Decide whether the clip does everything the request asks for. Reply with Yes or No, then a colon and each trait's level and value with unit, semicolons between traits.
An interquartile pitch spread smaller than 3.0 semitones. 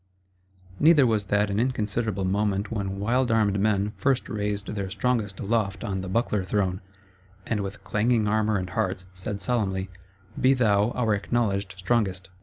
Yes: narrow, 2.6 semitones